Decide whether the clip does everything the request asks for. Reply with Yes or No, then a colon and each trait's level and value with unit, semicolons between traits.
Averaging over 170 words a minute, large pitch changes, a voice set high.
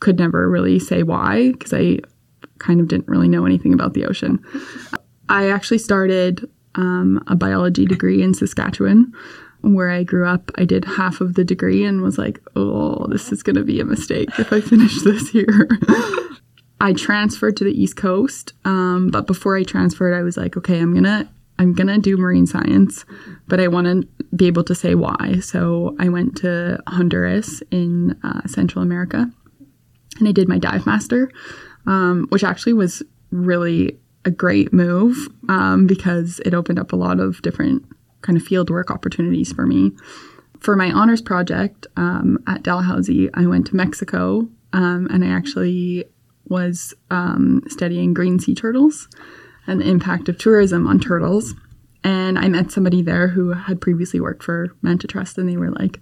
No: average, 180 wpm; wide, 8.1 semitones; medium, 180 Hz